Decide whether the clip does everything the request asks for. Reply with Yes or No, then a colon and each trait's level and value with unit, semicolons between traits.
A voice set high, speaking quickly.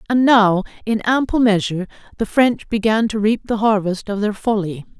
No: high, 215 Hz; average, 180 wpm